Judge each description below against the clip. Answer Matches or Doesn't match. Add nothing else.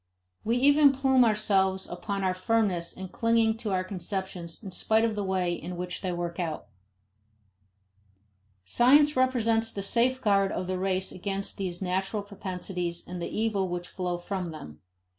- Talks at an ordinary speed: Matches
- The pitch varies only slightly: Doesn't match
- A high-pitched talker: Matches